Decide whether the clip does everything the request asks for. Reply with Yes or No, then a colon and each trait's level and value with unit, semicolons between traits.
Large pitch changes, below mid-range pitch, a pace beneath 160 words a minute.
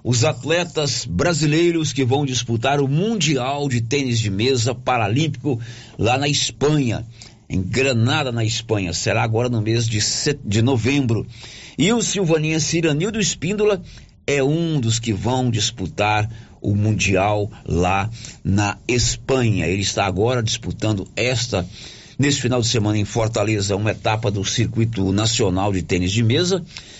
No: average, 4.8 semitones; low, 120 Hz; average, 140 wpm